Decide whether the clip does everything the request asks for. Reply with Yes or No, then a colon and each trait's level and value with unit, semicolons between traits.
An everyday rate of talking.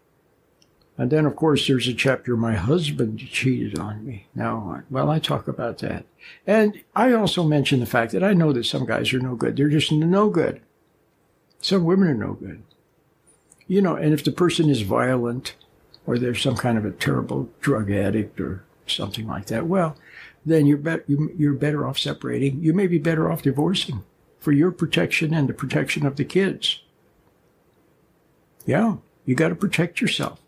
Yes: average, 185 wpm